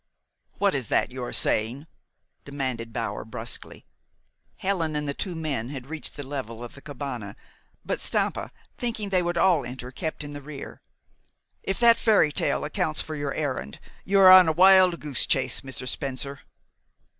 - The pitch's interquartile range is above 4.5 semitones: Yes, average, 5.1 semitones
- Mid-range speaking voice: Yes, medium, 145 Hz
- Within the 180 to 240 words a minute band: No, average, 170 wpm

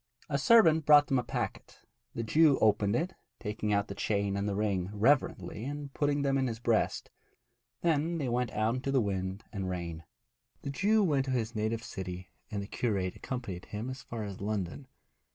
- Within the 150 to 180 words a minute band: No, average, 195 wpm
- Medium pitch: No, low, 115 Hz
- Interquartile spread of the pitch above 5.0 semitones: Yes, wide, 5.5 semitones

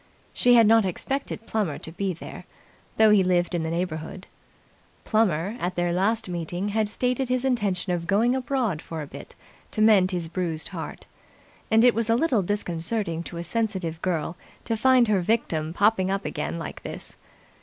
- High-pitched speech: Yes, high, 195 Hz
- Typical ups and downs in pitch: Yes, average, 4.6 semitones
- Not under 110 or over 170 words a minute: No, average, 180 wpm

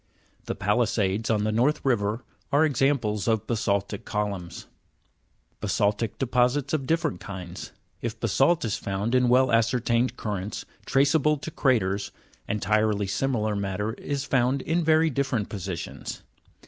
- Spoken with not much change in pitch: No, average, 4.7 semitones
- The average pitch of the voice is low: Yes, low, 115 Hz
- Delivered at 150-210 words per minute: No, slow, 135 wpm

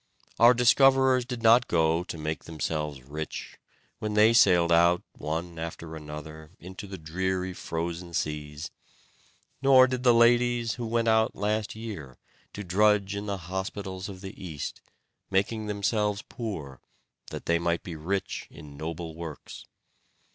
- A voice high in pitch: No, very low, 95 Hz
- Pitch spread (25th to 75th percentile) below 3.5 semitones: No, wide, 5.4 semitones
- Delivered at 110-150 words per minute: Yes, average, 145 wpm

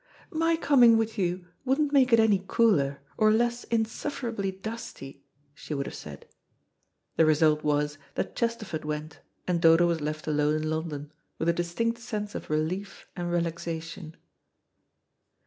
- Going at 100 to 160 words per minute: Yes, average, 145 wpm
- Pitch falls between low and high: Yes, medium, 175 Hz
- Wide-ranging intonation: Yes, wide, 6.7 semitones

